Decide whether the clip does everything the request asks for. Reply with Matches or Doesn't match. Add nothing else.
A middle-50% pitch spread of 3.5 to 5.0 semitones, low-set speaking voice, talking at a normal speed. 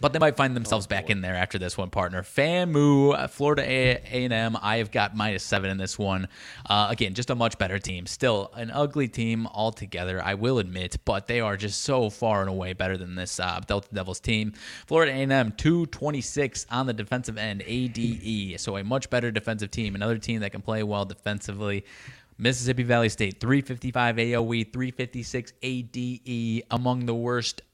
Matches